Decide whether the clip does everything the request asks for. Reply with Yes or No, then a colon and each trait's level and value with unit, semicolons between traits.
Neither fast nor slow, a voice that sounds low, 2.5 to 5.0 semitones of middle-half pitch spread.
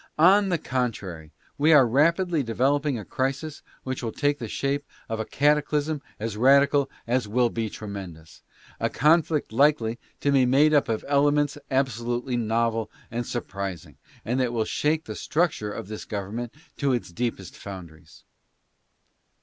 Yes: average, 160 wpm; low, 125 Hz; average, 4.6 semitones